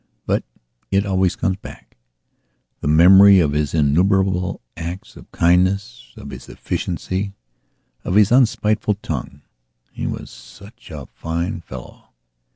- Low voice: Yes, very low, 95 Hz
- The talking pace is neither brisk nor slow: No, slow, 120 wpm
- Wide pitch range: No, average, 3.5 semitones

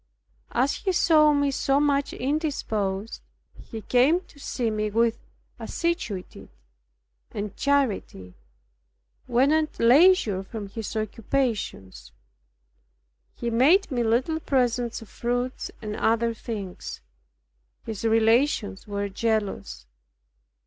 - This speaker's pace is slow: Yes, slow, 105 wpm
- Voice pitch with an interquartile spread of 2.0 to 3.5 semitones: No, average, 4.9 semitones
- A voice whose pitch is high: Yes, high, 235 Hz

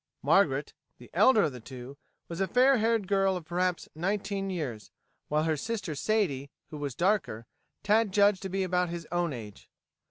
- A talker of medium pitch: Yes, medium, 180 Hz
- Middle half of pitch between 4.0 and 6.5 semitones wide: Yes, average, 5.2 semitones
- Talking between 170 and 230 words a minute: Yes, average, 180 wpm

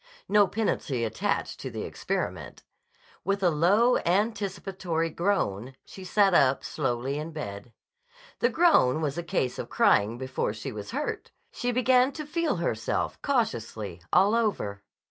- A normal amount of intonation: No, wide, 8.8 semitones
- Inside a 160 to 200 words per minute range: No, average, 145 wpm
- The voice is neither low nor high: Yes, medium, 170 Hz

